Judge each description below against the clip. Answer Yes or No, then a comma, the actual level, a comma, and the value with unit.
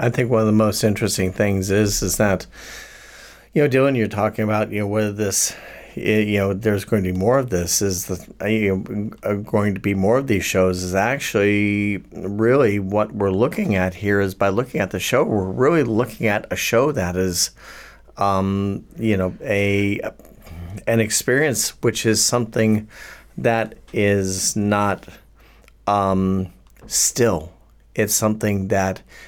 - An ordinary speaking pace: Yes, average, 160 wpm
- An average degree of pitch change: No, narrow, 2.1 semitones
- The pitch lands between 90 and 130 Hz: Yes, low, 105 Hz